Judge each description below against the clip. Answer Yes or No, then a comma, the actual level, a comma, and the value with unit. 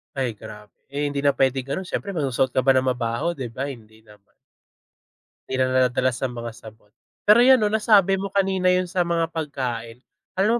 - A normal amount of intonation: No, wide, 7.2 semitones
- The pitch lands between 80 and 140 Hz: Yes, low, 135 Hz